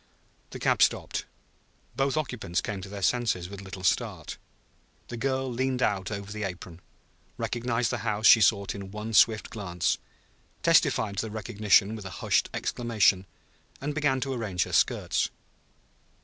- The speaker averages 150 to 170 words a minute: Yes, average, 160 wpm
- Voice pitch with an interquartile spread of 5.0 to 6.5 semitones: No, average, 3.7 semitones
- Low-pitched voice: Yes, low, 105 Hz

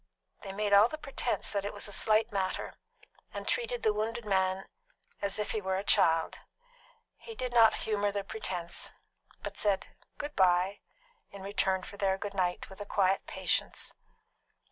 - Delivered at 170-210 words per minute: Yes, average, 175 wpm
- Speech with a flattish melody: Yes, narrow, 2.2 semitones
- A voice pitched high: Yes, high, 200 Hz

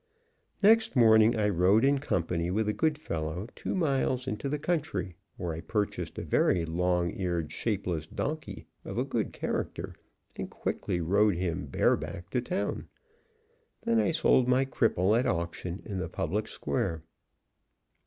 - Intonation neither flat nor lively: No, wide, 7.1 semitones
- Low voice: Yes, low, 105 Hz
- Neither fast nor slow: Yes, average, 155 wpm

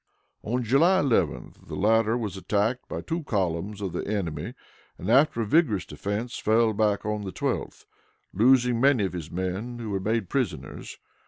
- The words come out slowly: No, average, 170 wpm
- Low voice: Yes, low, 110 Hz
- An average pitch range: Yes, average, 3.9 semitones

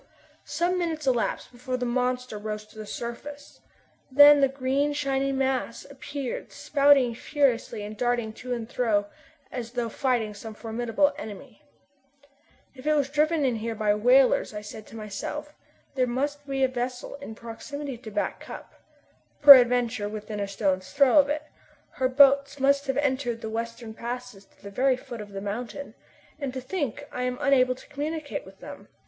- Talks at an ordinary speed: Yes, average, 175 wpm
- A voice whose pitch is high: Yes, very high, 250 Hz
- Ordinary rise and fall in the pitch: Yes, average, 3.7 semitones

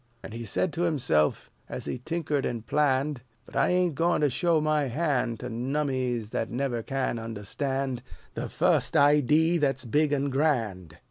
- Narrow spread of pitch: No, average, 4.1 semitones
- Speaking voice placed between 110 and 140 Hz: Yes, low, 135 Hz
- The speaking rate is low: No, average, 165 wpm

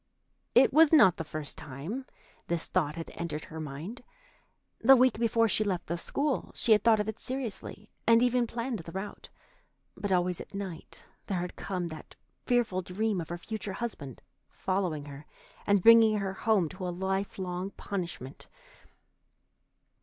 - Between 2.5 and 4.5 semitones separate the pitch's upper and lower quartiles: No, average, 4.9 semitones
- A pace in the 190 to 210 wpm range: No, average, 165 wpm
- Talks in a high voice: Yes, high, 195 Hz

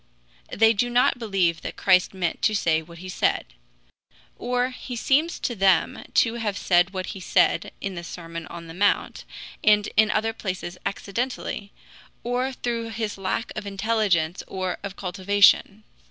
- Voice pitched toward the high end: Yes, high, 200 Hz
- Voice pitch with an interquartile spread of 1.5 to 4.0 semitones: Yes, average, 3.7 semitones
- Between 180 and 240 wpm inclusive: No, average, 160 wpm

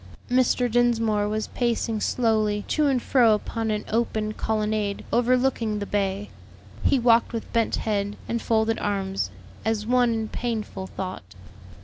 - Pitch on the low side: No, high, 220 Hz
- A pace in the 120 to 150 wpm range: Yes, average, 140 wpm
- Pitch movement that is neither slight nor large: No, narrow, 2.3 semitones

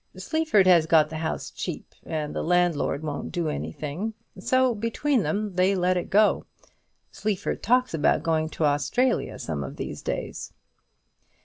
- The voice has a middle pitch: Yes, medium, 180 Hz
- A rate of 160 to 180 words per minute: No, average, 150 wpm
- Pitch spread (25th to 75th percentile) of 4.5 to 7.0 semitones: Yes, wide, 5.5 semitones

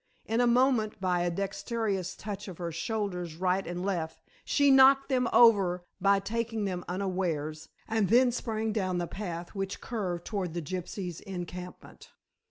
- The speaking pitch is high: Yes, high, 195 Hz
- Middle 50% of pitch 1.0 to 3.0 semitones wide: No, average, 4.0 semitones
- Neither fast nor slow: Yes, average, 160 wpm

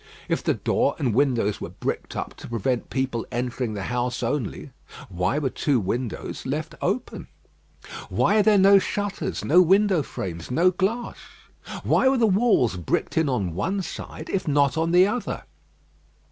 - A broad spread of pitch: Yes, wide, 8.2 semitones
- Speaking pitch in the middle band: Yes, medium, 145 Hz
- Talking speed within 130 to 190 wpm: Yes, average, 165 wpm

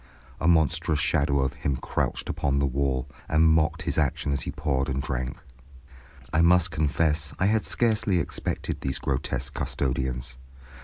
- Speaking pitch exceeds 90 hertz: No, very low, 70 Hz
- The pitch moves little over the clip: No, average, 3.2 semitones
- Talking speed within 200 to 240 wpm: No, average, 155 wpm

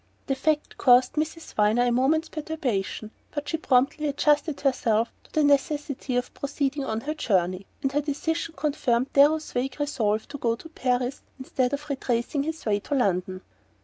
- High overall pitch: Yes, very high, 270 Hz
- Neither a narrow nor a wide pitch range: Yes, average, 3.7 semitones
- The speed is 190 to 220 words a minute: No, average, 170 wpm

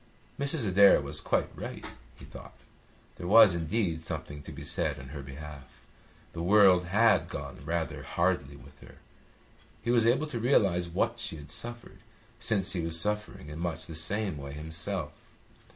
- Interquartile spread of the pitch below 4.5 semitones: No, wide, 5.5 semitones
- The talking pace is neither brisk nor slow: Yes, average, 170 wpm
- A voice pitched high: No, very low, 85 Hz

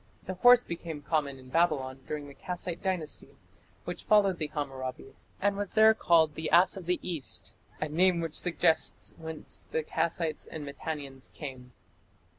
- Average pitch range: Yes, average, 3.6 semitones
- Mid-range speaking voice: Yes, medium, 160 Hz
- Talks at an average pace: Yes, average, 160 wpm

